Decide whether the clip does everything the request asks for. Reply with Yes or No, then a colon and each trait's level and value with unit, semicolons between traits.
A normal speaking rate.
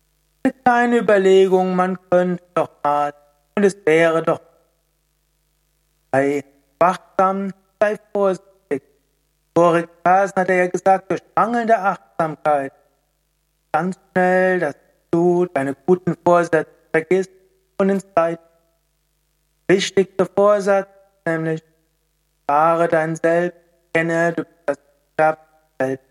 No: slow, 100 wpm